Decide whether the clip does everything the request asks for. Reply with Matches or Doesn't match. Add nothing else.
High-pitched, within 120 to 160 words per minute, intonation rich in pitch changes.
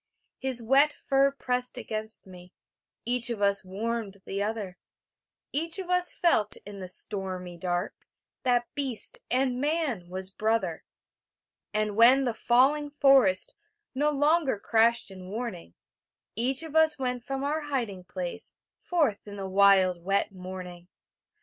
Matches